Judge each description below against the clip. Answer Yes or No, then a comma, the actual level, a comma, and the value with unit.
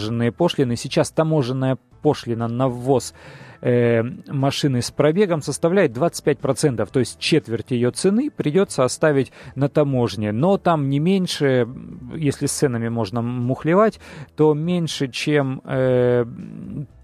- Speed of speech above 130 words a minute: No, average, 125 wpm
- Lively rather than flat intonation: No, average, 4.1 semitones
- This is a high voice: No, medium, 140 Hz